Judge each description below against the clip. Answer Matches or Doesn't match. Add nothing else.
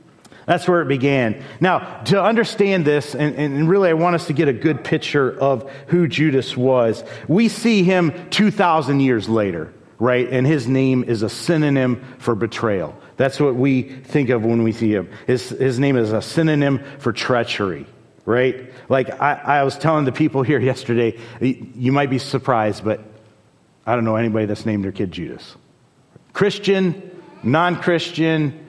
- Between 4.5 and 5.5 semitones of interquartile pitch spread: Matches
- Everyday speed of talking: Matches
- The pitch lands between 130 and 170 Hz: Matches